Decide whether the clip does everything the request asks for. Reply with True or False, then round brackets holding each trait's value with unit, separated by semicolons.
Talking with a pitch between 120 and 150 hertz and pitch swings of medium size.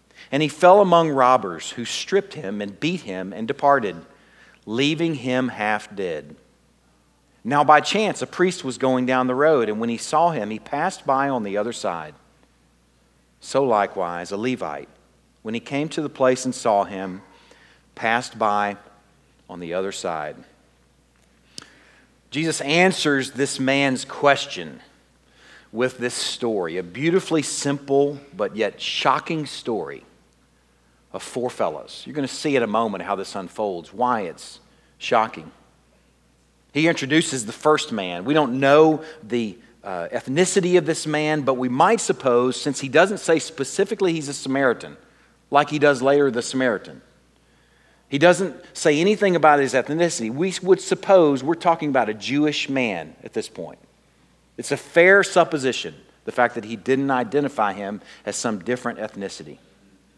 False (135 Hz; 6.4 semitones)